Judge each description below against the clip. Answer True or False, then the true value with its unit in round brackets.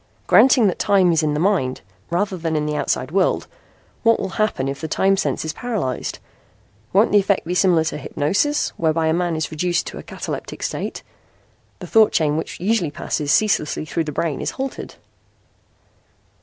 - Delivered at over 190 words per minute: False (185 wpm)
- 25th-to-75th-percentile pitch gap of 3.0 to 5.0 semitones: True (4.5 semitones)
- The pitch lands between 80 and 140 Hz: False (170 Hz)